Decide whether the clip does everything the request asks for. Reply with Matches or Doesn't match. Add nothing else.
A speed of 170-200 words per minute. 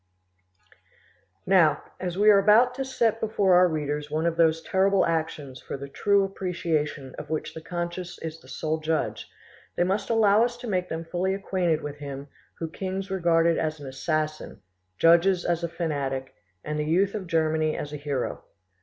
Matches